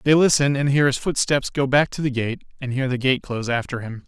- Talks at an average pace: No, fast, 265 wpm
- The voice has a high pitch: No, low, 135 Hz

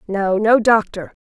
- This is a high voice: Yes, high, 210 Hz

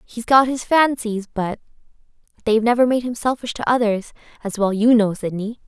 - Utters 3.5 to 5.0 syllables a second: No, 5.4 syllables/s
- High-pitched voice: Yes, high, 225 Hz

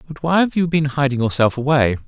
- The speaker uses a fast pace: Yes, fast, 230 wpm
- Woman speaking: No, male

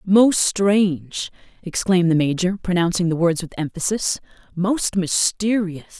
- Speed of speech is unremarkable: No, slow, 110 wpm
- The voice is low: No, medium, 185 Hz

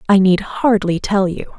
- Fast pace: No, average, 190 wpm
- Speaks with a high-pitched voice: Yes, high, 195 Hz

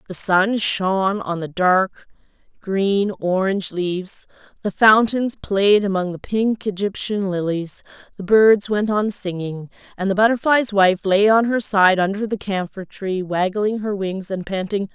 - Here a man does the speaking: No, female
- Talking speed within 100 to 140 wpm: No, average, 175 wpm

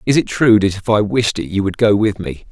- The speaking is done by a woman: No, male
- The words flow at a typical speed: No, fast, 310 wpm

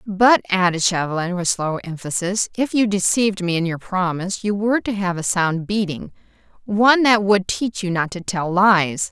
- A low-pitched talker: No, high, 190 Hz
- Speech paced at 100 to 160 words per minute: No, average, 190 wpm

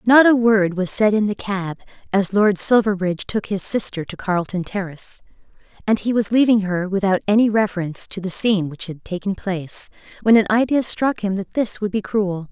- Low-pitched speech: No, high, 200 Hz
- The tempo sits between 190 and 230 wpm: Yes, average, 200 wpm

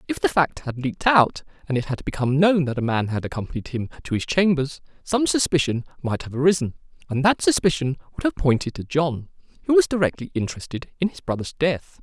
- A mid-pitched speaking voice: Yes, medium, 150 Hz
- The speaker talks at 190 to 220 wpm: Yes, fast, 205 wpm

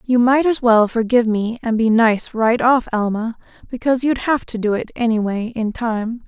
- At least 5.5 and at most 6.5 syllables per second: No, 4.9 syllables/s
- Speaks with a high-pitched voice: Yes, high, 230 Hz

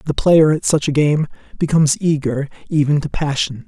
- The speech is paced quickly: No, average, 180 wpm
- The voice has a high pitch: No, medium, 150 Hz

